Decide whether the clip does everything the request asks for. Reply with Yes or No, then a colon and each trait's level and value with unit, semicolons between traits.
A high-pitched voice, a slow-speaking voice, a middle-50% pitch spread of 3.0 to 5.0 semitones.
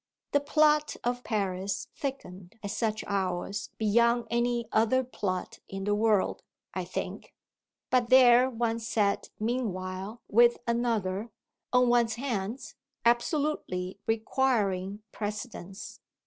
Yes: high, 225 Hz; slow, 110 wpm; average, 3.5 semitones